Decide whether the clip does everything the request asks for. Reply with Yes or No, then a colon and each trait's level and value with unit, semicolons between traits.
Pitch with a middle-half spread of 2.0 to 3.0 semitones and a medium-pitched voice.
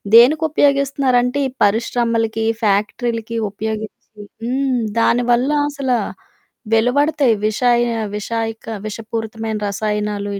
No: narrow, 2.6 semitones; high, 230 Hz